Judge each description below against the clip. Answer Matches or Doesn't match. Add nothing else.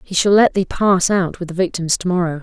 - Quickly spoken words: Matches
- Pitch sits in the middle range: Matches